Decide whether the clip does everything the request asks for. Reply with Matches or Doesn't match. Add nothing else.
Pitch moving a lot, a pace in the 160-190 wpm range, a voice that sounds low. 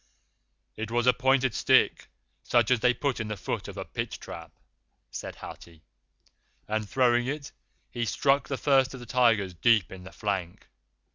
Doesn't match